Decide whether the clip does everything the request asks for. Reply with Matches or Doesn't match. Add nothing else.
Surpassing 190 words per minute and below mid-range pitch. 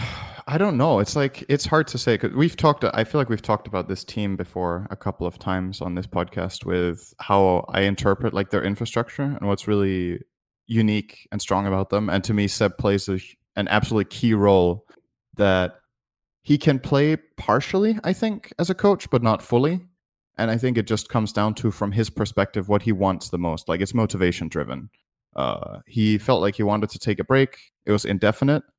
Matches